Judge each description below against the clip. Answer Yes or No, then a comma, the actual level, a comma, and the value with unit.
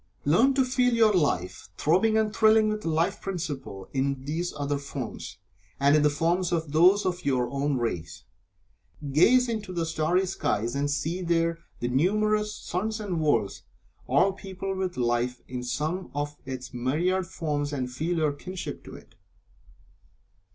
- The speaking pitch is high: No, medium, 160 Hz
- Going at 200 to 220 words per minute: No, average, 160 wpm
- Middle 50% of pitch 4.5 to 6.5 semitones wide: Yes, average, 5.3 semitones